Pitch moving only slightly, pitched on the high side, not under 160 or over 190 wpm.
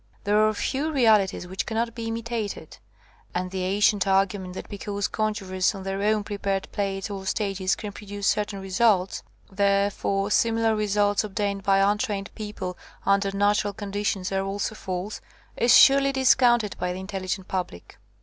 Yes: narrow, 1.9 semitones; high, 200 Hz; average, 170 wpm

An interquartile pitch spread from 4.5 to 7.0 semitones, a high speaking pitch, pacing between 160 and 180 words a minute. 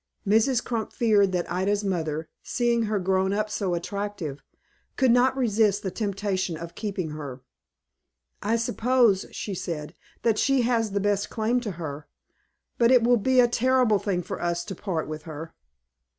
Yes: average, 4.8 semitones; high, 205 Hz; average, 165 wpm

